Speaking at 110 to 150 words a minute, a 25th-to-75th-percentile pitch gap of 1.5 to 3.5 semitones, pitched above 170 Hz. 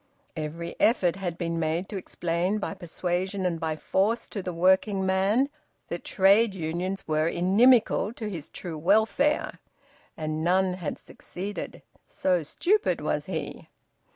Yes: average, 140 wpm; average, 3.1 semitones; medium, 185 Hz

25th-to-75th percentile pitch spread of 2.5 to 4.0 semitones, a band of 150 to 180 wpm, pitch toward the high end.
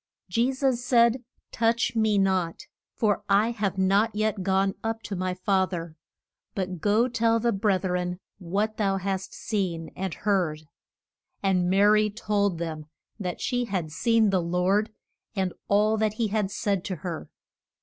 Yes: average, 2.9 semitones; average, 160 wpm; high, 200 Hz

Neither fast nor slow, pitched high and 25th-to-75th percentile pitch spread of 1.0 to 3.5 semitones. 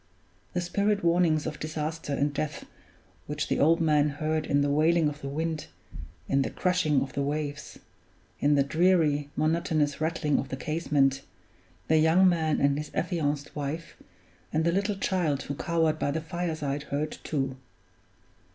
No: average, 160 wpm; medium, 155 Hz; narrow, 2.5 semitones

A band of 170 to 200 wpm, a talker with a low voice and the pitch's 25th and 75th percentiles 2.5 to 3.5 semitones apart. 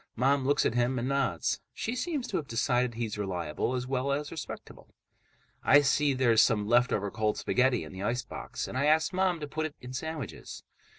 No: average, 195 wpm; low, 130 Hz; average, 3.9 semitones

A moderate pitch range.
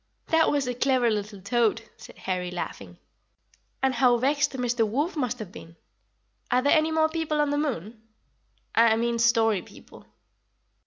Yes: average, 4.6 semitones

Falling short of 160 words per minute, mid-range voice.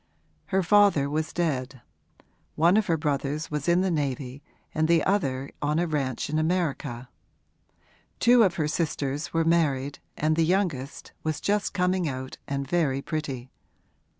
Yes: average, 150 wpm; medium, 155 Hz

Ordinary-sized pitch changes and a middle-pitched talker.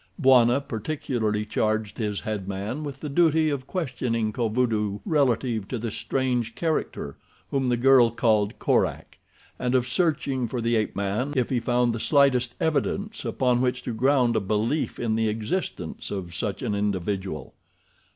No: average, 3.8 semitones; low, 120 Hz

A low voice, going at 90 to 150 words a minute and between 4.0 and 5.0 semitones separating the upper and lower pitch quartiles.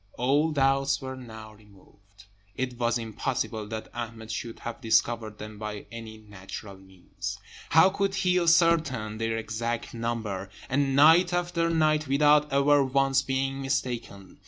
Yes: low, 125 Hz; average, 140 wpm; average, 4.7 semitones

